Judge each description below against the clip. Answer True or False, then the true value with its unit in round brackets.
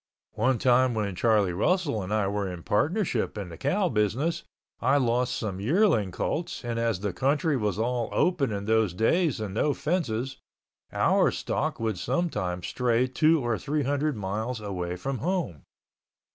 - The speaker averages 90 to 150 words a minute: False (165 wpm)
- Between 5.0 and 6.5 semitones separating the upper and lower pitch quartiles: True (5.6 semitones)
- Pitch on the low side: True (115 Hz)